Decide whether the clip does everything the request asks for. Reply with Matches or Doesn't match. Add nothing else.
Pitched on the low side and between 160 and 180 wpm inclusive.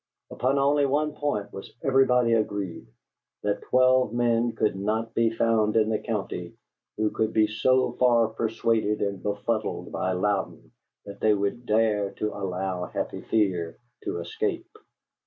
Doesn't match